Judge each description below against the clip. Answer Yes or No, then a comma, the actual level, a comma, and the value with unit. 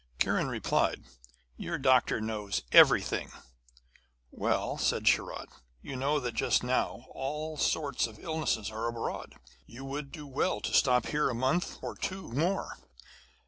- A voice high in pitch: No, low, 135 Hz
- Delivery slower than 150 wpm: Yes, average, 140 wpm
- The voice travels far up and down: No, average, 4.3 semitones